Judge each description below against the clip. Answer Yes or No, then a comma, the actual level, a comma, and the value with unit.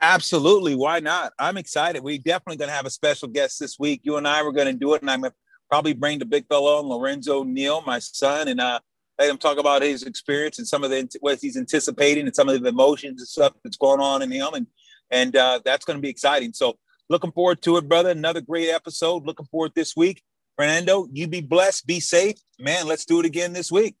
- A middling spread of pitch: Yes, average, 3.5 semitones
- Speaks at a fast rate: Yes, fast, 245 wpm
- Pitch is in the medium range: Yes, medium, 150 Hz